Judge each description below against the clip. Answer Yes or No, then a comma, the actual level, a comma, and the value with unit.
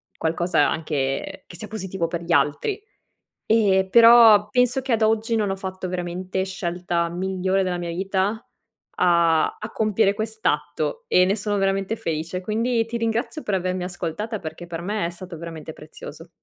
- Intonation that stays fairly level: No, average, 4.0 semitones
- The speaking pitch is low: No, high, 190 Hz